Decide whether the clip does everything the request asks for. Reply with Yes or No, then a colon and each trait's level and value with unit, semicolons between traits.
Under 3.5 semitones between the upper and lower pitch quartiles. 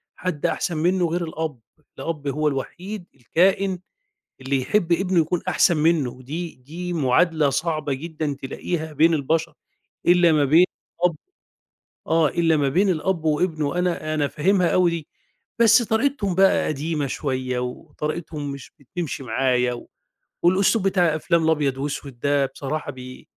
No: average, 3.8 semitones